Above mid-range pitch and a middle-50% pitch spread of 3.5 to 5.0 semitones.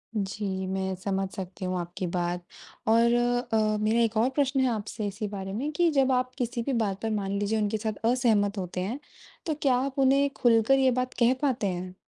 Yes: high, 220 Hz; average, 4.7 semitones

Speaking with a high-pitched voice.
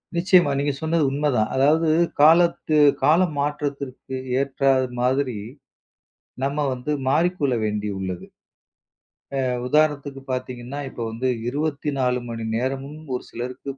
No: medium, 140 Hz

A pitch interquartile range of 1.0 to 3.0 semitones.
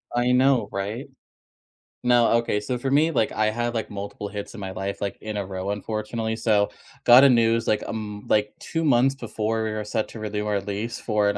Yes: narrow, 2.5 semitones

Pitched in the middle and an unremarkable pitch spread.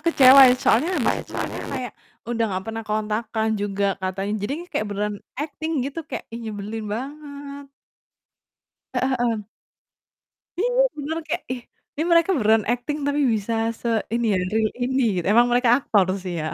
No: high, 235 Hz; average, 5.0 semitones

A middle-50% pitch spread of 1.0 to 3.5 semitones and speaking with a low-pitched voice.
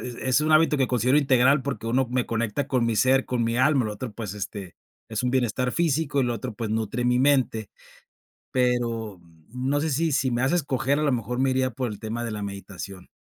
Yes: average, 2.9 semitones; low, 125 Hz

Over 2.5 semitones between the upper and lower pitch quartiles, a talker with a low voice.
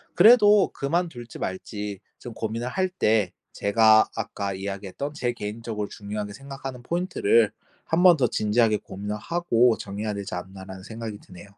Yes: average, 5.3 semitones; low, 110 Hz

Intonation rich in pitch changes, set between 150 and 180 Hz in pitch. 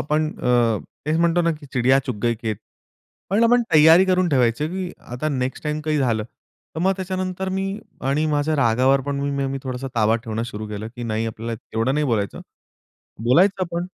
No: wide, 6.1 semitones; medium, 140 Hz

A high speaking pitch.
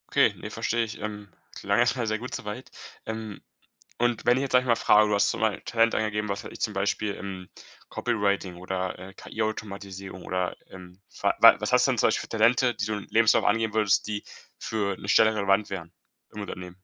No: low, 105 Hz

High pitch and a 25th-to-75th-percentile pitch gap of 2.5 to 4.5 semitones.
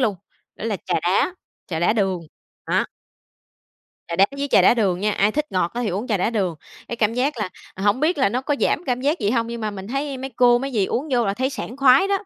No: high, 235 Hz; average, 5.0 semitones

